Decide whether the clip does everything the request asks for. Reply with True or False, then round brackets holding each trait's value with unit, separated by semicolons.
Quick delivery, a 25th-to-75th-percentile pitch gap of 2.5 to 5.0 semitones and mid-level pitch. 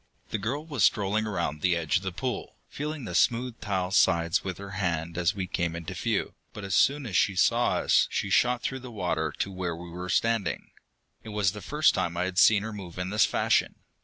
False (225 wpm; 4.1 semitones; 95 Hz)